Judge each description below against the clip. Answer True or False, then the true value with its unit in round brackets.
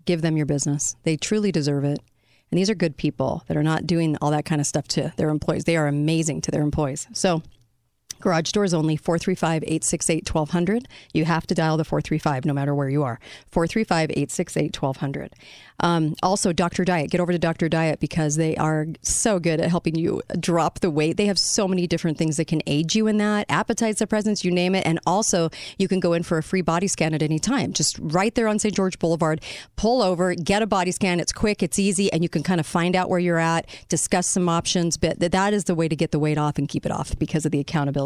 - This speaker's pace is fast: True (235 wpm)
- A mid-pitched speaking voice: True (165 Hz)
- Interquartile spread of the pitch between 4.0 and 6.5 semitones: False (3.2 semitones)